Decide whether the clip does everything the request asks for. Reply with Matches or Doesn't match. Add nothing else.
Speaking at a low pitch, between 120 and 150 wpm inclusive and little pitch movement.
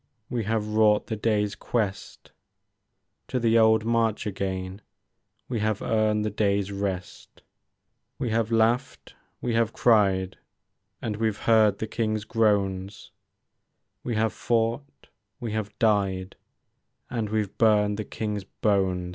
Matches